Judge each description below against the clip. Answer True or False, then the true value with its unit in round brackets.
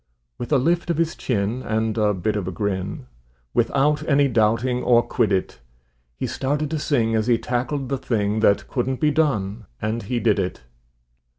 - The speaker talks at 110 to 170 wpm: False (180 wpm)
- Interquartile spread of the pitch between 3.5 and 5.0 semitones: True (4.6 semitones)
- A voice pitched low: True (120 Hz)